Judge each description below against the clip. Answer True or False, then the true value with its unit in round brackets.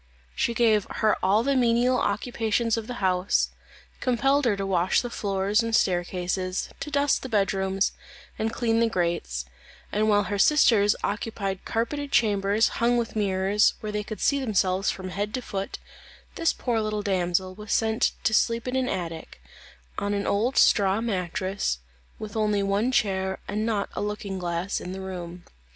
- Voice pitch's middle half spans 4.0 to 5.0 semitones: False (3.2 semitones)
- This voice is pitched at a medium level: False (205 Hz)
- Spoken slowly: False (170 wpm)